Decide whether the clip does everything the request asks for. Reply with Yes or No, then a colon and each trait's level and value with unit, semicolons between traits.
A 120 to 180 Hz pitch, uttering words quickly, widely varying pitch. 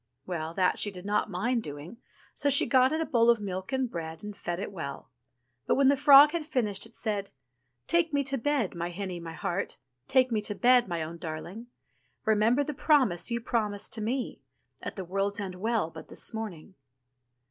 No: high, 210 Hz; fast, 210 wpm; wide, 5.8 semitones